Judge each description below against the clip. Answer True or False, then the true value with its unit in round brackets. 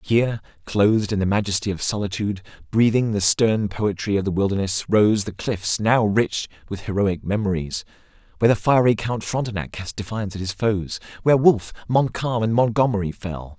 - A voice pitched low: True (105 Hz)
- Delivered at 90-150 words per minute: False (170 wpm)